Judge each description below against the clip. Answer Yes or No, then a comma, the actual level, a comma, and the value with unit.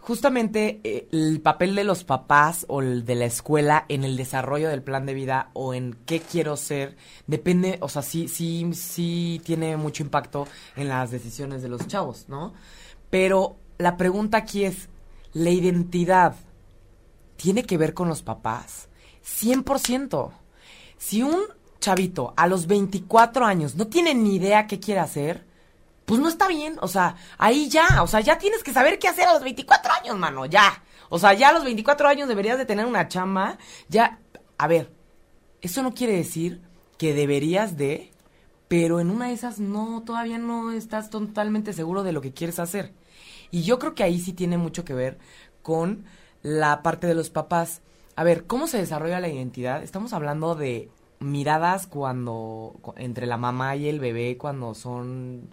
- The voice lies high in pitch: No, medium, 170 Hz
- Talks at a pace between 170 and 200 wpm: Yes, average, 175 wpm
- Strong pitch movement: Yes, wide, 6.7 semitones